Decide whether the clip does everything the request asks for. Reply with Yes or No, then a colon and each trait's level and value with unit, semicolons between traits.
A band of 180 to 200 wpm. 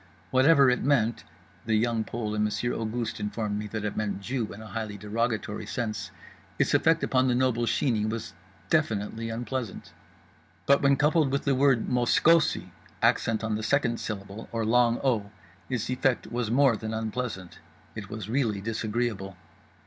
No: average, 160 wpm